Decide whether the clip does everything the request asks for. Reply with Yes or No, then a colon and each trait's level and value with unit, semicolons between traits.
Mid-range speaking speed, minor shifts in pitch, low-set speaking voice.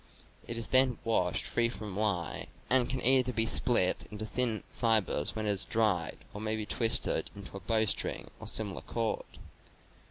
Yes: average, 170 wpm; narrow, 2.3 semitones; low, 110 Hz